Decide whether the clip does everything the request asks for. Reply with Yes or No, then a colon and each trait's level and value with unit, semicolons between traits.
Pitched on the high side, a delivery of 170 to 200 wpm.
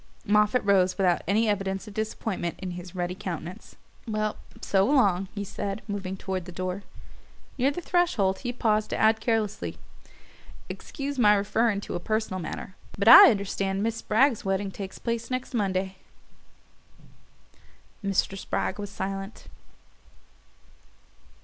No: high, 200 Hz; slow, 135 wpm